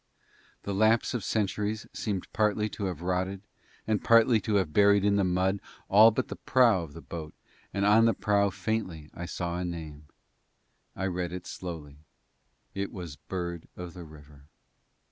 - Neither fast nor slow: Yes, average, 170 wpm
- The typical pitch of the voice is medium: No, very low, 95 Hz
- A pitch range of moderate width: Yes, average, 3.3 semitones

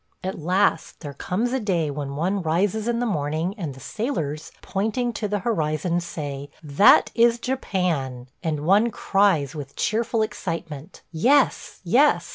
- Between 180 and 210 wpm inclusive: No, average, 150 wpm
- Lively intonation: Yes, wide, 6.2 semitones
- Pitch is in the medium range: Yes, medium, 180 Hz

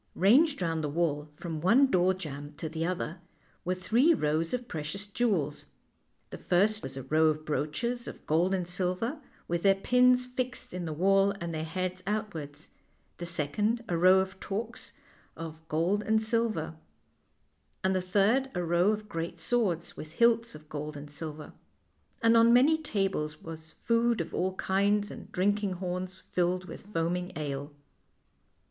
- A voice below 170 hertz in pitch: No, medium, 185 Hz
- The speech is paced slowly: No, average, 165 wpm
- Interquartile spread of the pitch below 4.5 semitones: No, average, 5.0 semitones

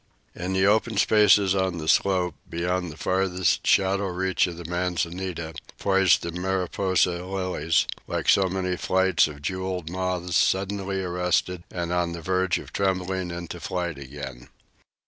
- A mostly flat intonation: Yes, narrow, 1.5 semitones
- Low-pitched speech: Yes, very low, 90 Hz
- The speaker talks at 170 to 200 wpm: No, average, 145 wpm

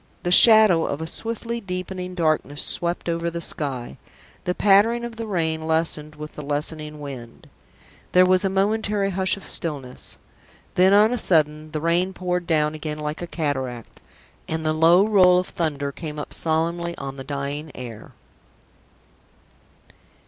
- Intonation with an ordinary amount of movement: Yes, average, 3.6 semitones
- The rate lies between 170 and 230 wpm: No, average, 155 wpm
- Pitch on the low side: No, medium, 165 Hz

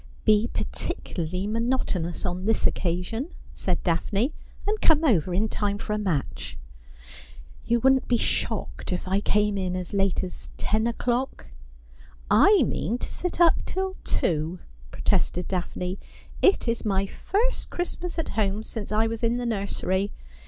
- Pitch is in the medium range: No, high, 210 Hz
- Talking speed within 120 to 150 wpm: No, average, 165 wpm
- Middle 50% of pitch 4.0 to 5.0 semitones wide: Yes, average, 4.7 semitones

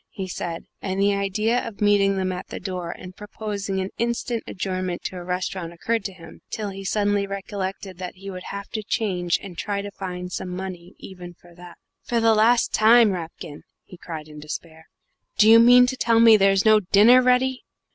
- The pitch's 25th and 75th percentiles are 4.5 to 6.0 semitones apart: No, average, 3.1 semitones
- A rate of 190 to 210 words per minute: Yes, average, 200 wpm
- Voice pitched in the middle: No, high, 195 Hz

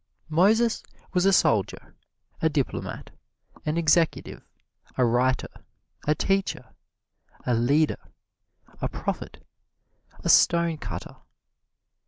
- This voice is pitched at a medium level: Yes, medium, 160 Hz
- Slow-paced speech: Yes, slow, 90 wpm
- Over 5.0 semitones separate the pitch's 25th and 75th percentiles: Yes, wide, 5.6 semitones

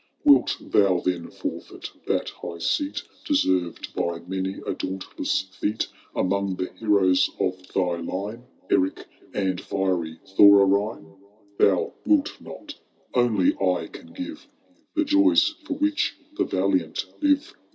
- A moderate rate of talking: No, slow, 130 wpm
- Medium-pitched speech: No, low, 100 Hz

